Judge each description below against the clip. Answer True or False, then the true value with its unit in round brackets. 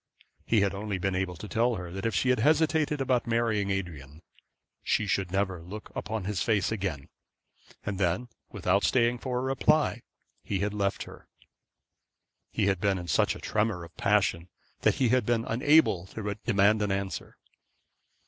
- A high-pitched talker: False (105 Hz)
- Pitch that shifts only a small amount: False (3.6 semitones)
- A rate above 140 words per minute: True (170 wpm)